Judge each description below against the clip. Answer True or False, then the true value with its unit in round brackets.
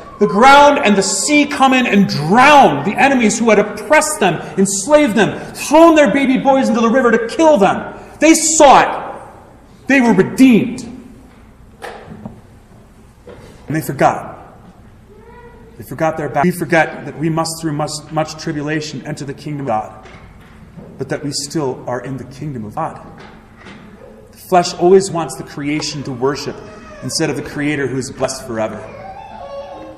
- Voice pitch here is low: False (165 Hz)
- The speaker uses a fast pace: False (160 wpm)